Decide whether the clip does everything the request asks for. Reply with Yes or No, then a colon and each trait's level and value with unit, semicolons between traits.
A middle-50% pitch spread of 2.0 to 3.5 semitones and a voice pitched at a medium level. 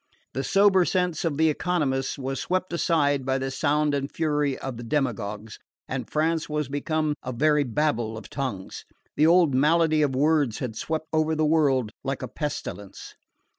Yes: average, 3.0 semitones; medium, 145 Hz